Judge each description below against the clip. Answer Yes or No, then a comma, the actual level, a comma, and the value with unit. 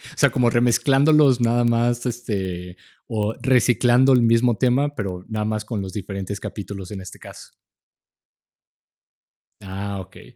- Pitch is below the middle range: Yes, low, 115 Hz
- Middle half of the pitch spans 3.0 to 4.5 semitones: Yes, average, 3.6 semitones